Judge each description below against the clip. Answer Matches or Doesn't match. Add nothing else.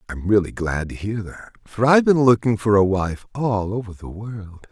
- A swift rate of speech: Matches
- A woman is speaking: Doesn't match